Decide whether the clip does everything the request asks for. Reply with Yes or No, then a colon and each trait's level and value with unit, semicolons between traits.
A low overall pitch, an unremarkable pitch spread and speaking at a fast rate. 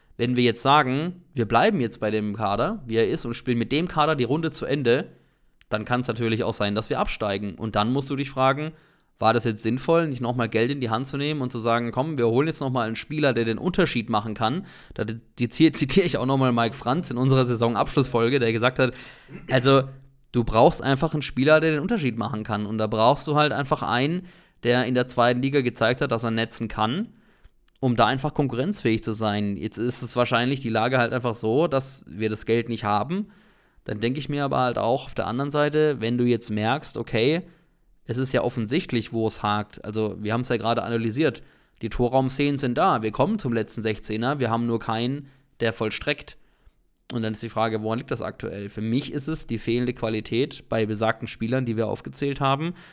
Yes: low, 120 Hz; average, 3.8 semitones; fast, 220 wpm